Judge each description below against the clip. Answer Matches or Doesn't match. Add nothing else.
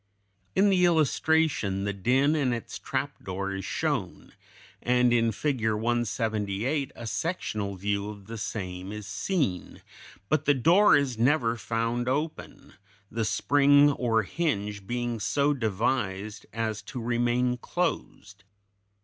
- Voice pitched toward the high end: Doesn't match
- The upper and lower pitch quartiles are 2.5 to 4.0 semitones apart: Doesn't match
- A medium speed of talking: Doesn't match